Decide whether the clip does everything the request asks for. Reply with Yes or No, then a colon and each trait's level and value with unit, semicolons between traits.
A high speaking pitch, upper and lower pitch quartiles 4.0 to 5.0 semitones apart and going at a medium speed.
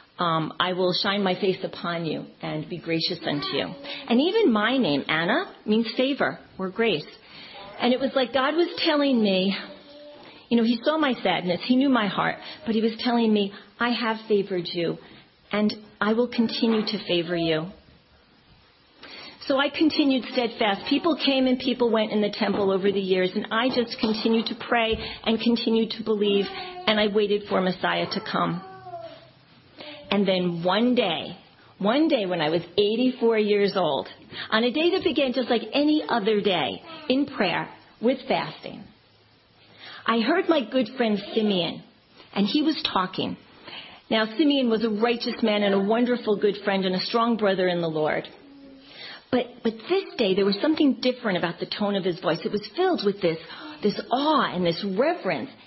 Yes: high, 225 Hz; average, 4.6 semitones; average, 180 wpm